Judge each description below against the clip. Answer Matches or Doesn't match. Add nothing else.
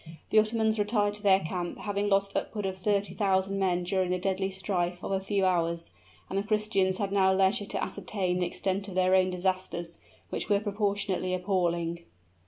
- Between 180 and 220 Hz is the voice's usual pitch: Matches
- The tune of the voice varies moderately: Doesn't match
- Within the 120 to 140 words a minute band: Doesn't match